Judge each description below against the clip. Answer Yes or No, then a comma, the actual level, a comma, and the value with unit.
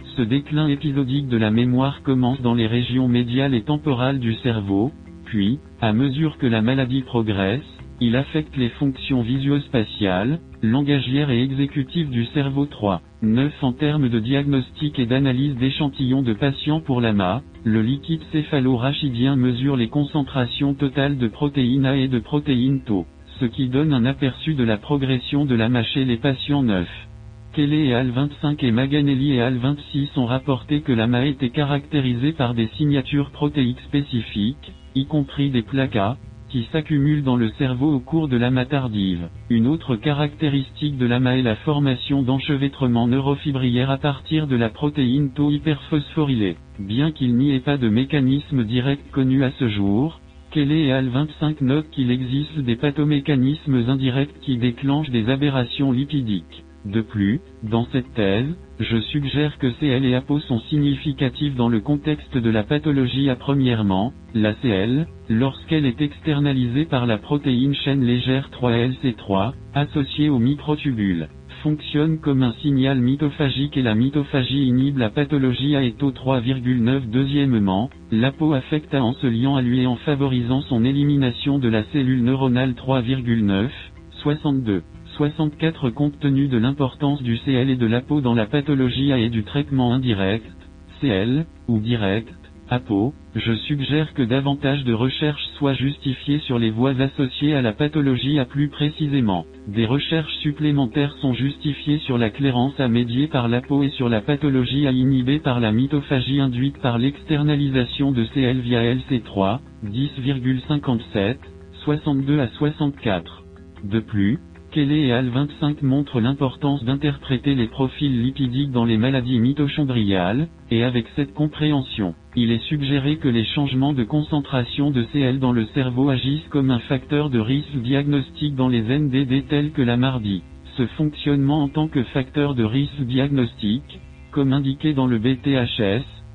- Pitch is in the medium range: No, low, 130 Hz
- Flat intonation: No, average, 3.2 semitones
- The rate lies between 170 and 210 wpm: No, average, 155 wpm